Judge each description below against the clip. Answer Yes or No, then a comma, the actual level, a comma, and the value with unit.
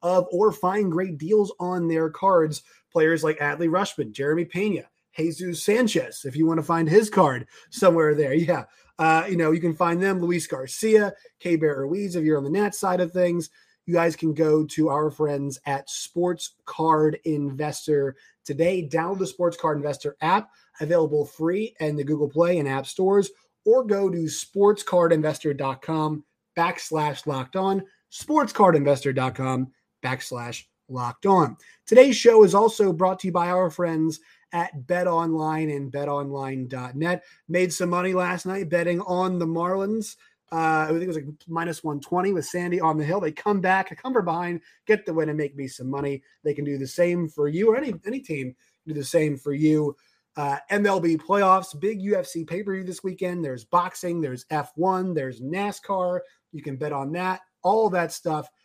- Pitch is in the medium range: Yes, medium, 170 Hz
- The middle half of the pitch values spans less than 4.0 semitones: Yes, average, 3.5 semitones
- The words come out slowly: No, average, 180 wpm